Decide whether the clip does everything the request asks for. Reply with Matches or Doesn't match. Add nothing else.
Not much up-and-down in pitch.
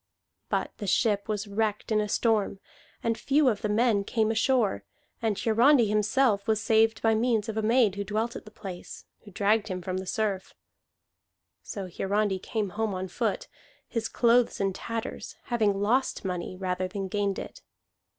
Matches